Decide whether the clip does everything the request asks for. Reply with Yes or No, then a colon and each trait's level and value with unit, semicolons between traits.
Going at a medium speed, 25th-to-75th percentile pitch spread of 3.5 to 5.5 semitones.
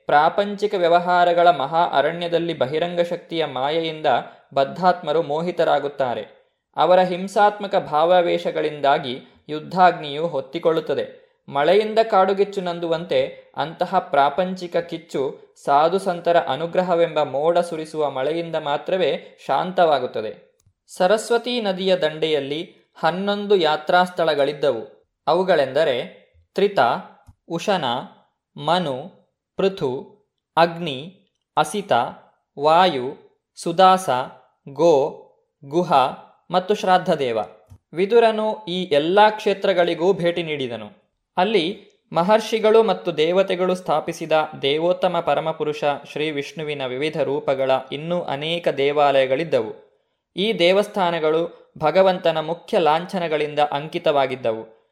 Yes: average, 80 wpm; average, 4.3 semitones